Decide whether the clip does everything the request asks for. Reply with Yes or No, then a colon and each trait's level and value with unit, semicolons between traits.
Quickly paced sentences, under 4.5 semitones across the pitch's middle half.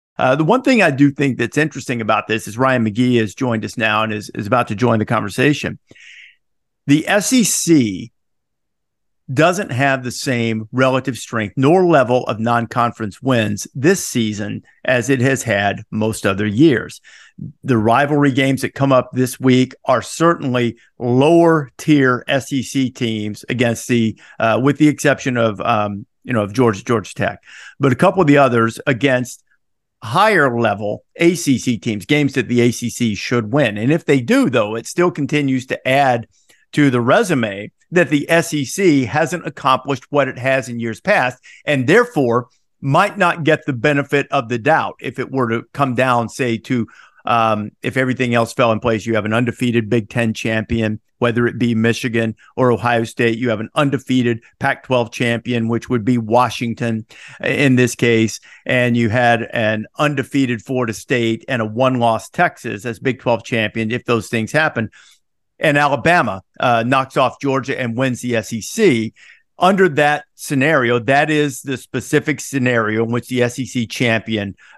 No: average, 170 wpm; average, 3.4 semitones